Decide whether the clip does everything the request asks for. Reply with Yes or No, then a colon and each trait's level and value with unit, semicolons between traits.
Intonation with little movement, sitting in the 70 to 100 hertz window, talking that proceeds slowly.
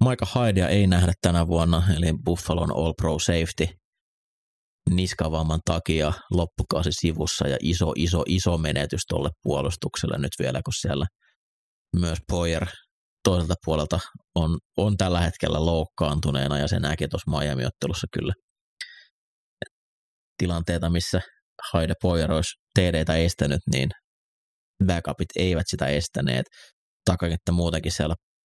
No: narrow, 2.2 semitones; very low, 85 Hz; average, 120 wpm